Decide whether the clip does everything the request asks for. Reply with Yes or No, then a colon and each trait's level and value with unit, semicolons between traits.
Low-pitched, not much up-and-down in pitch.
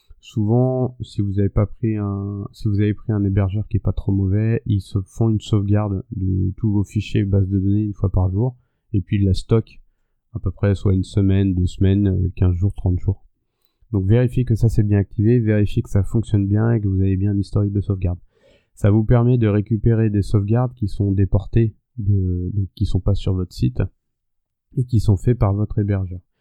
Yes: low, 100 Hz; narrow, 2.3 semitones